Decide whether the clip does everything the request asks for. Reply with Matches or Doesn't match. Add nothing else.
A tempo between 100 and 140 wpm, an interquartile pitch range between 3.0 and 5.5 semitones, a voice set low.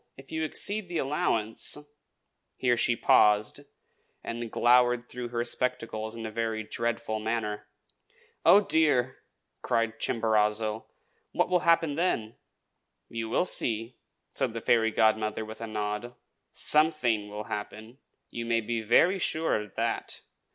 Doesn't match